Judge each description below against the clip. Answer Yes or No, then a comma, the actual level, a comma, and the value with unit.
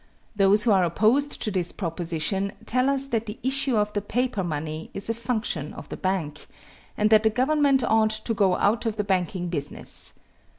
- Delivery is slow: No, average, 185 wpm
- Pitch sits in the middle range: No, high, 210 Hz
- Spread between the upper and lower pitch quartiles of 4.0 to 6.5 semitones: Yes, average, 4.3 semitones